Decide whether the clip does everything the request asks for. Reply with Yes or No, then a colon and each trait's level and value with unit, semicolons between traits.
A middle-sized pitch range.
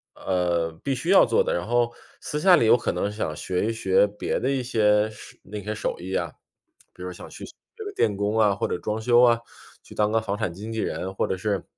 Yes: average, 3.8 semitones